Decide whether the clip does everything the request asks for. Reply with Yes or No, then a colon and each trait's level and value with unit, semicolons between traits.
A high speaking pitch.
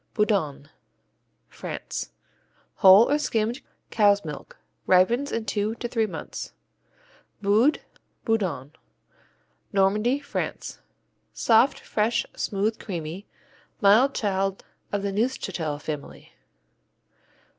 Yes: high, 205 Hz